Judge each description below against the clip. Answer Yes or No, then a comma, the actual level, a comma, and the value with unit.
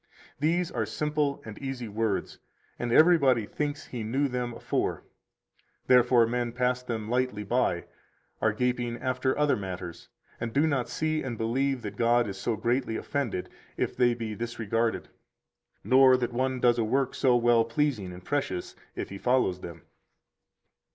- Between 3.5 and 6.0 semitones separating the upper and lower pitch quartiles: No, average, 2.7 semitones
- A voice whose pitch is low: Yes, low, 120 Hz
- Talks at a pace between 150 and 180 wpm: Yes, average, 160 wpm